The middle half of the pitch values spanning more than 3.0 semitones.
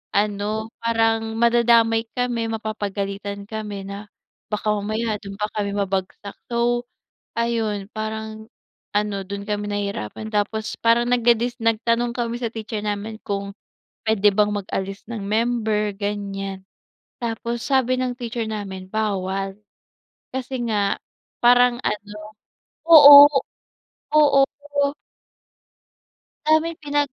No: narrow, 2.5 semitones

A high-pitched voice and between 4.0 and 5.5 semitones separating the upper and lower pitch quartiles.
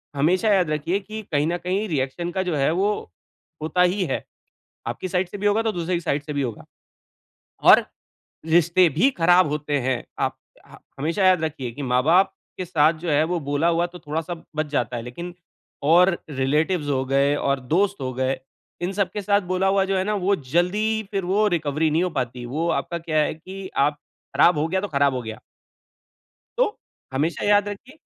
No: medium, 170 Hz; average, 4.6 semitones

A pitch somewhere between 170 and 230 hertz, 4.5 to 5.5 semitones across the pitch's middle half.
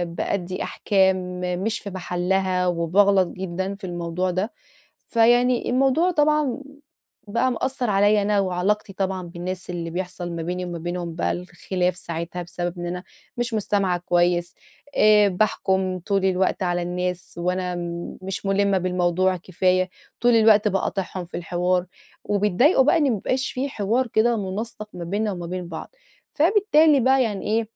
No: high, 190 Hz; average, 3.2 semitones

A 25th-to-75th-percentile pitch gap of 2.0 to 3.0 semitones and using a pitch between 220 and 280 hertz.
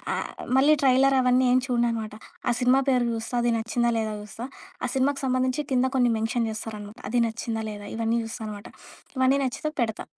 Yes: narrow, 2.5 semitones; high, 240 Hz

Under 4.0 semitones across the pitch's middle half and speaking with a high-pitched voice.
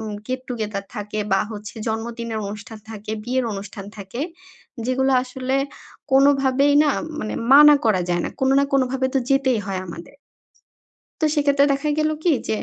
No: average, 4.3 semitones; high, 245 Hz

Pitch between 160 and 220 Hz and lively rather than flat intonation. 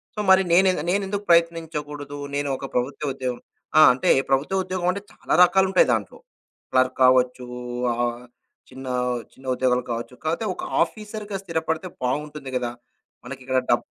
No: medium, 145 Hz; wide, 6.2 semitones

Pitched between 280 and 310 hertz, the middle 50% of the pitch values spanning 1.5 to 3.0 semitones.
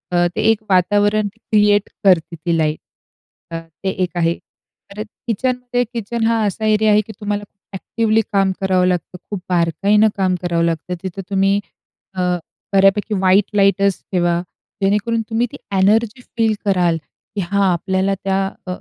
No: high, 195 Hz; narrow, 2.6 semitones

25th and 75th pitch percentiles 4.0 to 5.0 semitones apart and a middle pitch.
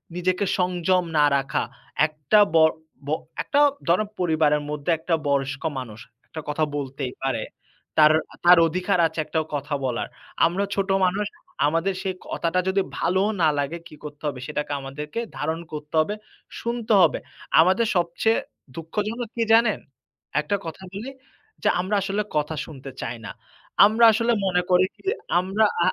Yes: average, 4.6 semitones; medium, 170 Hz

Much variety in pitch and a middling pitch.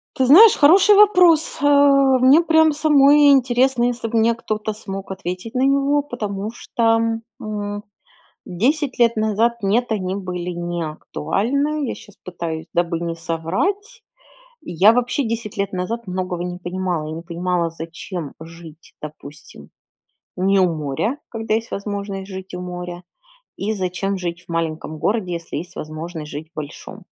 No: wide, 6.2 semitones; high, 200 Hz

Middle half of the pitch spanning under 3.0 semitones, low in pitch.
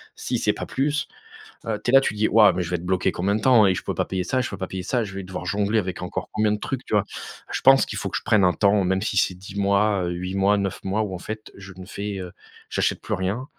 Yes: narrow, 2.4 semitones; low, 100 Hz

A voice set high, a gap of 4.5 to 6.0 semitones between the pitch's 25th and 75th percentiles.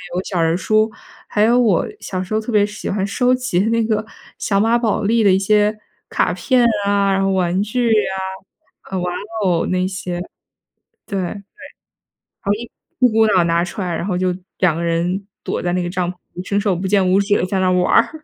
No: high, 195 Hz; average, 3.0 semitones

